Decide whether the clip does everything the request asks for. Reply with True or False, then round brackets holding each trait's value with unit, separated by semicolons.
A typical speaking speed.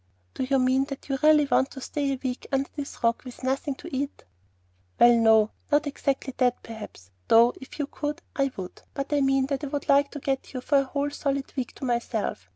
False (225 wpm)